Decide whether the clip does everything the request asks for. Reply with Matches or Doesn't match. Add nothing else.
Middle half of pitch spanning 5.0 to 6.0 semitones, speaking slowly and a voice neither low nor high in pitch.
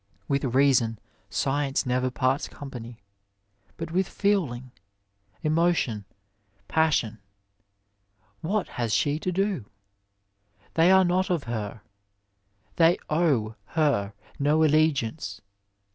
Matches